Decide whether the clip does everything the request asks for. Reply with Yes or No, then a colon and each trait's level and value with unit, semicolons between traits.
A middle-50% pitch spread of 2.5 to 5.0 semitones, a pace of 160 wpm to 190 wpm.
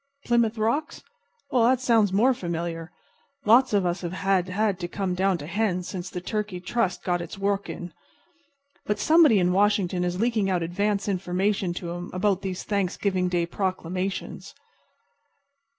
No: average, 2.9 semitones; average, 150 wpm